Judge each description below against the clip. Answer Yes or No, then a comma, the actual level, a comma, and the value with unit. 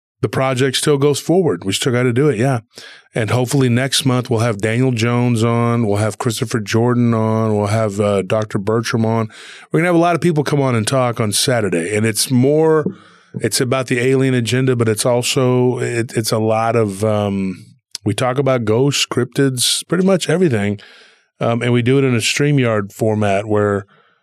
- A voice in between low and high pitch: No, low, 120 Hz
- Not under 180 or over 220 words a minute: Yes, fast, 205 wpm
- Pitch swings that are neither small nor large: Yes, average, 3.2 semitones